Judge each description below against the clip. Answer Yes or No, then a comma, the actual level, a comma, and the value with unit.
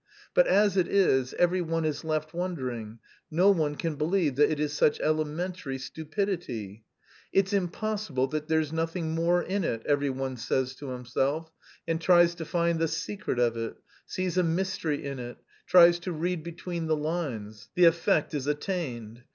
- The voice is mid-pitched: Yes, medium, 160 Hz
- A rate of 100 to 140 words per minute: No, average, 170 wpm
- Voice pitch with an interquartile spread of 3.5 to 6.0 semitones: Yes, average, 4.2 semitones